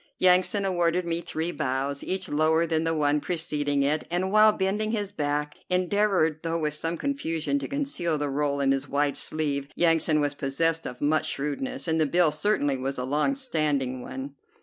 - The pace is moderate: Yes, average, 185 wpm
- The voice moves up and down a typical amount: Yes, average, 3.8 semitones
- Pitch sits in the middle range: Yes, medium, 155 Hz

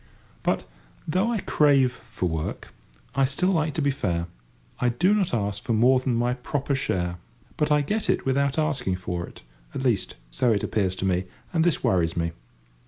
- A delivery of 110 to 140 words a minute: No, average, 180 wpm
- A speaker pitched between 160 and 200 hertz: No, low, 125 Hz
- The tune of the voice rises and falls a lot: Yes, wide, 8.1 semitones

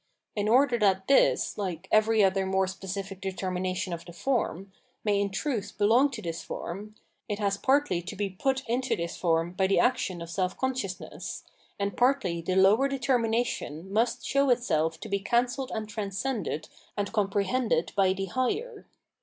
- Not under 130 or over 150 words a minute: No, average, 170 wpm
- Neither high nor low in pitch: No, high, 200 Hz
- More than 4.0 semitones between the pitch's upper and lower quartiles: Yes, average, 4.4 semitones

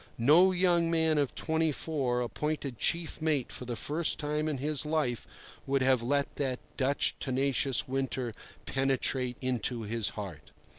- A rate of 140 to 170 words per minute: Yes, average, 150 wpm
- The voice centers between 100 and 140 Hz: Yes, low, 135 Hz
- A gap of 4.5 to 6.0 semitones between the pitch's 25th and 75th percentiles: No, average, 3.7 semitones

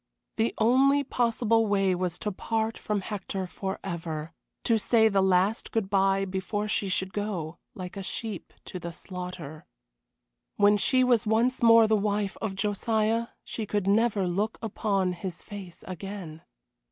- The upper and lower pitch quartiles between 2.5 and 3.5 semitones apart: Yes, average, 3.0 semitones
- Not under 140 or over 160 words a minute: Yes, average, 155 wpm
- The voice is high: Yes, high, 205 Hz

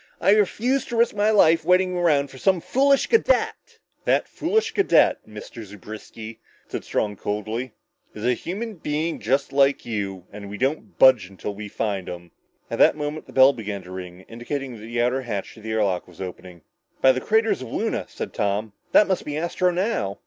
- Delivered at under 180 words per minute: No, average, 190 wpm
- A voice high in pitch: No, low, 130 Hz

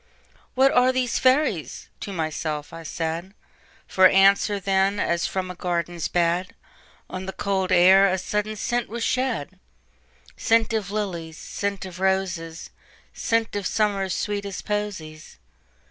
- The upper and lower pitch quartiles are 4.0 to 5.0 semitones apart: No, average, 3.5 semitones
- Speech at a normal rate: No, slow, 120 wpm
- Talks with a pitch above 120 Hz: Yes, high, 190 Hz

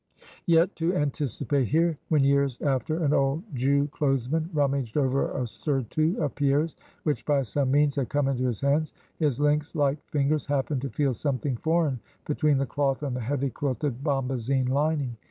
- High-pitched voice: No, medium, 140 Hz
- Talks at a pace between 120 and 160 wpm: No, average, 175 wpm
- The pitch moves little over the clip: Yes, narrow, 2.0 semitones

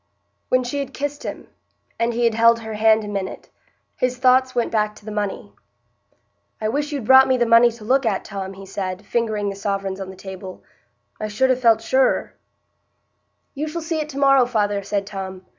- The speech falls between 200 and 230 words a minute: Yes, fast, 205 wpm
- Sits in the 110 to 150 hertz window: No, high, 225 Hz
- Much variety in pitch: No, average, 4.3 semitones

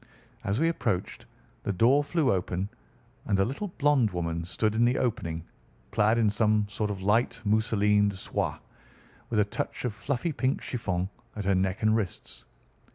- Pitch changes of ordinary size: Yes, average, 3.6 semitones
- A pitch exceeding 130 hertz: No, low, 105 Hz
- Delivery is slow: No, average, 170 wpm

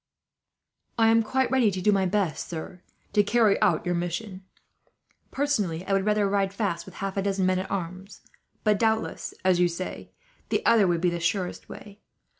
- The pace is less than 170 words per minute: No, average, 190 wpm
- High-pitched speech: Yes, high, 195 Hz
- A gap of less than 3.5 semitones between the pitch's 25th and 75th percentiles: Yes, average, 2.8 semitones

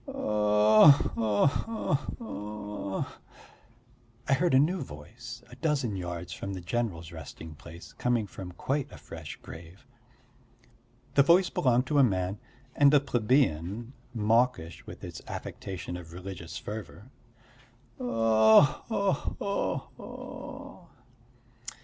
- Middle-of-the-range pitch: No, low, 110 Hz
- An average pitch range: No, wide, 6.2 semitones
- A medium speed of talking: No, slow, 120 wpm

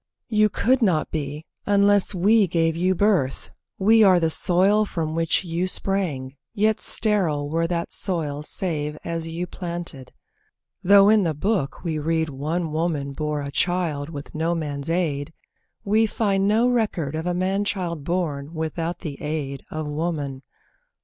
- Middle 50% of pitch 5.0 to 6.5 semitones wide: No, average, 4.3 semitones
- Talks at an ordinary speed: Yes, average, 155 wpm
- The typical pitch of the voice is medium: Yes, medium, 170 Hz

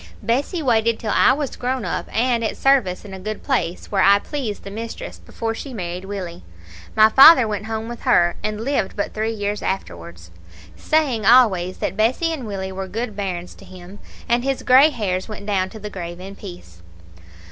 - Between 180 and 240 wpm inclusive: Yes, average, 195 wpm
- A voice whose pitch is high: Yes, high, 215 Hz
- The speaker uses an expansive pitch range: No, average, 4.2 semitones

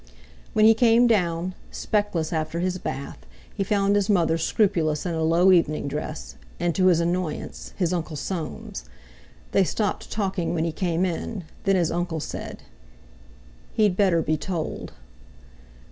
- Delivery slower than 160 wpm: Yes, average, 150 wpm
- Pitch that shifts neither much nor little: Yes, average, 3.3 semitones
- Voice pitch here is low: No, medium, 175 Hz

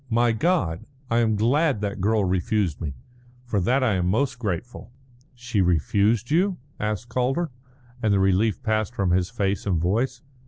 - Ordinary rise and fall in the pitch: Yes, average, 4.1 semitones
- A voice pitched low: Yes, low, 110 Hz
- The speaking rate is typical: Yes, average, 165 wpm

